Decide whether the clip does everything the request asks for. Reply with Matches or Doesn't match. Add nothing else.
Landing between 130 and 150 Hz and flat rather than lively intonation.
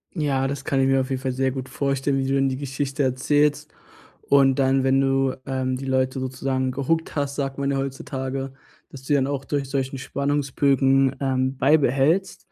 Matches